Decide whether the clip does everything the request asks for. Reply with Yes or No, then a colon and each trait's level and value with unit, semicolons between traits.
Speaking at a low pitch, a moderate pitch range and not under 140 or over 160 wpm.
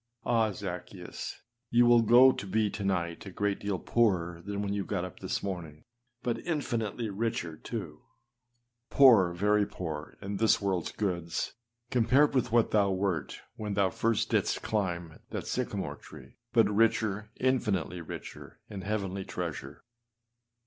Yes: low, 100 Hz; average, 3.8 semitones; average, 155 wpm